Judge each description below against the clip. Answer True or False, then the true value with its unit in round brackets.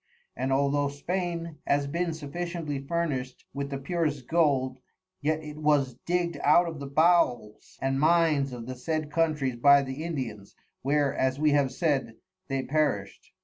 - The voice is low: False (145 Hz)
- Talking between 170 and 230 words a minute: False (155 wpm)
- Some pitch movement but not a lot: True (3.3 semitones)